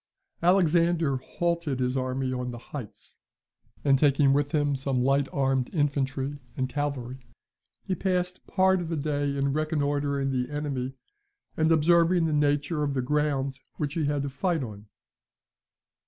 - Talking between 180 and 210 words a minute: No, average, 155 wpm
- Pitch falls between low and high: Yes, medium, 145 Hz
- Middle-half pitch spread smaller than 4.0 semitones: Yes, average, 2.7 semitones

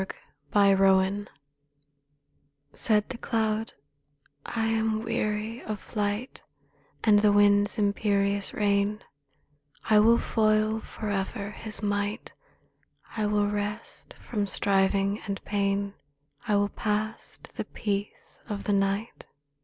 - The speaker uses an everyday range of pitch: No, narrow, 1.3 semitones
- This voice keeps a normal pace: No, slow, 115 wpm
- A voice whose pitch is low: No, high, 205 Hz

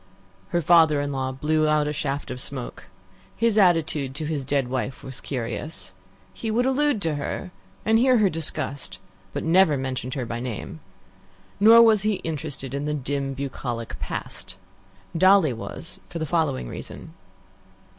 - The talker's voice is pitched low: No, medium, 150 Hz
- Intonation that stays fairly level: No, average, 4.7 semitones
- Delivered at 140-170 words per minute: Yes, average, 160 wpm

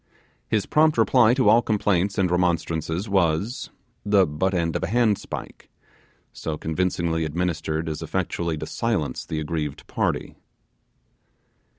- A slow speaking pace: Yes, slow, 125 wpm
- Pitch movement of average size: Yes, average, 4.4 semitones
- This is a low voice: Yes, very low, 90 Hz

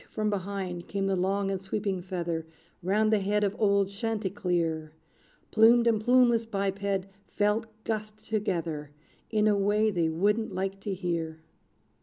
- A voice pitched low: No, high, 200 Hz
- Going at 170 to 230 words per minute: No, average, 145 wpm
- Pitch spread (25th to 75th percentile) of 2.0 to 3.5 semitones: Yes, average, 2.8 semitones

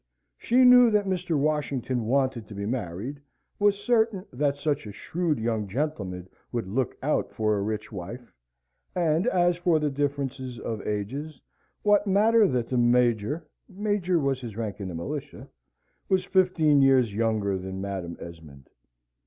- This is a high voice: No, low, 135 Hz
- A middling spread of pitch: No, wide, 8.3 semitones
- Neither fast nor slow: Yes, average, 155 wpm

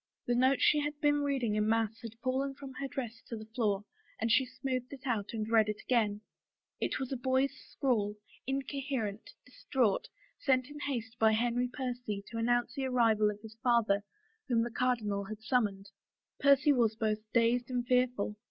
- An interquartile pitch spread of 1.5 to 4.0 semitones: Yes, average, 3.2 semitones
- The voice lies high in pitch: Yes, high, 240 Hz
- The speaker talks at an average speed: Yes, average, 180 wpm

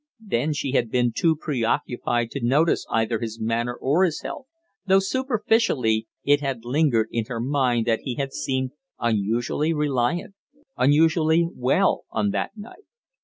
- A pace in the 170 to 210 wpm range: No, average, 150 wpm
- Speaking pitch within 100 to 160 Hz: Yes, low, 135 Hz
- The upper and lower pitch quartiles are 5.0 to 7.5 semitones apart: Yes, wide, 5.4 semitones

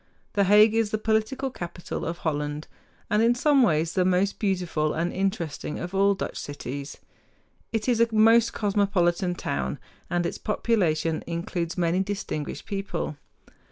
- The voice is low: No, high, 190 Hz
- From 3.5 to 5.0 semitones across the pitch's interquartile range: Yes, average, 4.3 semitones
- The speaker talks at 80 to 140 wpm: No, average, 150 wpm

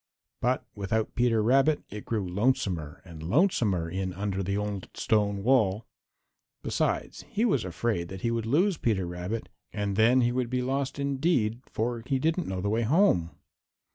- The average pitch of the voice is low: Yes, low, 110 Hz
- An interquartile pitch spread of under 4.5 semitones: No, average, 4.9 semitones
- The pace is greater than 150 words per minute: Yes, average, 170 wpm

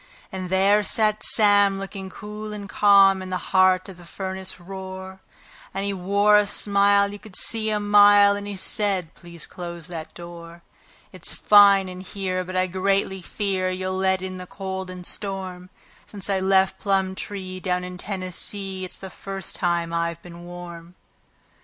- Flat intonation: Yes, narrow, 1.6 semitones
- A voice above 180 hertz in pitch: Yes, high, 190 Hz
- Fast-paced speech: No, average, 170 wpm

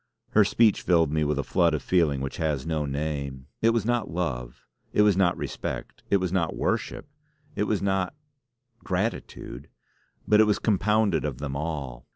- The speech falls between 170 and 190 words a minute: Yes, average, 180 wpm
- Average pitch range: No, wide, 6.1 semitones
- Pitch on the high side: No, very low, 85 Hz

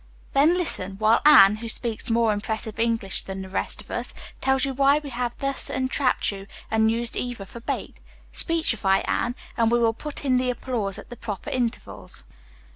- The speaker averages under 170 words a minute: No, average, 195 wpm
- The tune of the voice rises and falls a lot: No, average, 3.4 semitones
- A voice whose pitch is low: No, high, 235 Hz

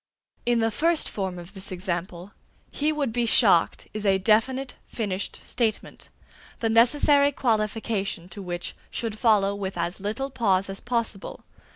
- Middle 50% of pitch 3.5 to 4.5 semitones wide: Yes, average, 3.8 semitones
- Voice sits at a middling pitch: No, high, 215 Hz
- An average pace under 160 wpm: Yes, average, 150 wpm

